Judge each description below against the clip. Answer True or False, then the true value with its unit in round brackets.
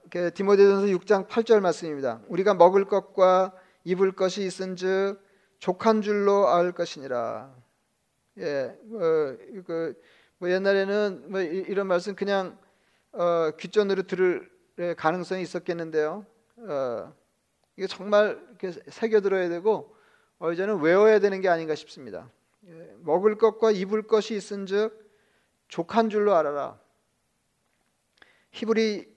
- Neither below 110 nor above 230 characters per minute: False (250 characters per minute)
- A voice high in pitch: True (195 Hz)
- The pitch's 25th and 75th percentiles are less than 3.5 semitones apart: True (2.8 semitones)